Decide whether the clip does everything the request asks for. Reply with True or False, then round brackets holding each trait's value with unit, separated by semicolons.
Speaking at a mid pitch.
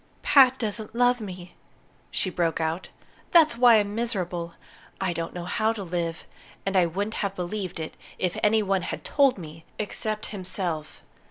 False (195 Hz)